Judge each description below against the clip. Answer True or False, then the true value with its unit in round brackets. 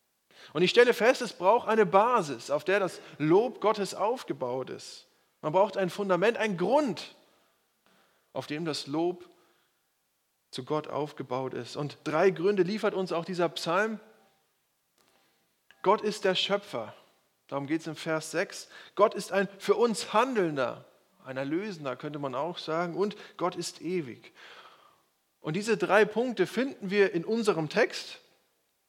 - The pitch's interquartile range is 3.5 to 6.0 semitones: True (4.9 semitones)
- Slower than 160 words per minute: True (150 wpm)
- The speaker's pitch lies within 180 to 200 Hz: True (185 Hz)